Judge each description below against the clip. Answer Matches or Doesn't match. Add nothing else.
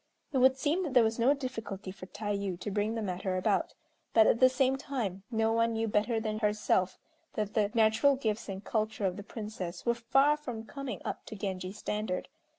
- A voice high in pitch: Matches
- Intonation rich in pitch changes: Doesn't match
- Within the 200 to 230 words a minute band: Matches